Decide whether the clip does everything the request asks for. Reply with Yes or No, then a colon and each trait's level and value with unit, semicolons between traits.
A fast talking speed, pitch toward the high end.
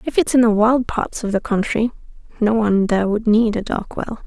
Yes: fast, 240 wpm; high, 220 Hz